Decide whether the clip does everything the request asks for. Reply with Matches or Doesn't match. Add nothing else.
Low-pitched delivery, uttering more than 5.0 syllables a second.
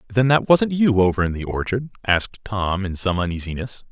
Matches